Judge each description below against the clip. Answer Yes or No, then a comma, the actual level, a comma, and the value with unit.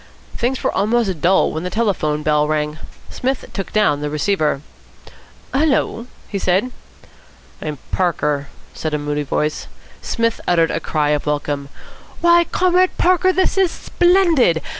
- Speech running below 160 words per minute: Yes, average, 140 wpm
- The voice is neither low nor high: Yes, medium, 180 Hz